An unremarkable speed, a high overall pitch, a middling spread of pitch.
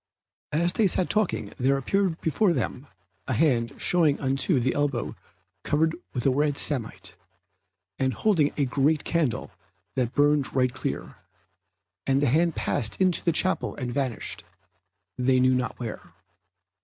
No: average, 145 wpm; medium, 140 Hz; average, 4.1 semitones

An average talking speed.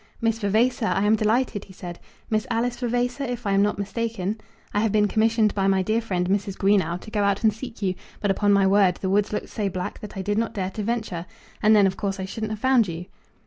No: fast, 250 wpm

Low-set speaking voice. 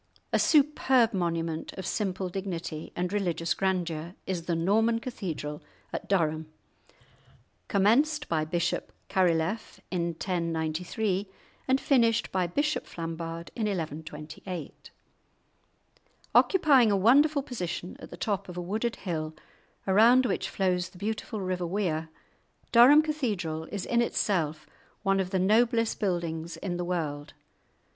No: medium, 185 Hz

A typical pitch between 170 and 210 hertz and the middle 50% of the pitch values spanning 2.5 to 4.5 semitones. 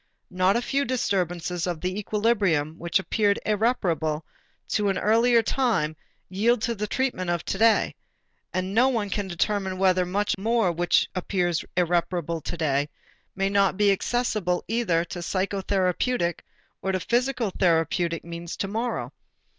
Yes: high, 190 Hz; average, 3.9 semitones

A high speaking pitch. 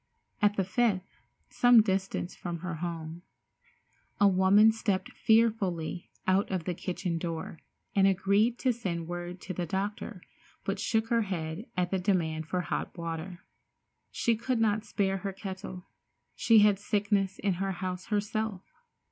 Yes: high, 195 Hz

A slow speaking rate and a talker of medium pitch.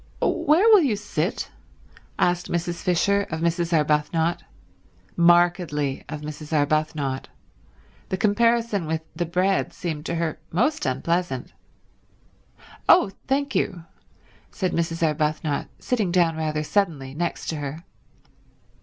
Yes: slow, 115 wpm; medium, 170 Hz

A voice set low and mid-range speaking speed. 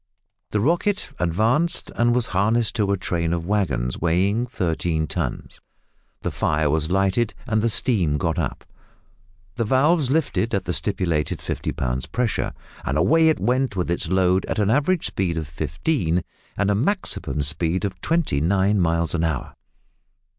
Yes: very low, 95 Hz; average, 160 wpm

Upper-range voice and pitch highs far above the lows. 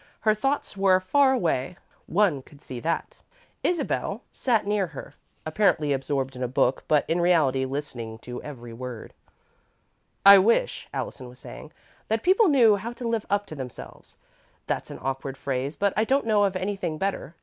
No: medium, 170 Hz; wide, 7.8 semitones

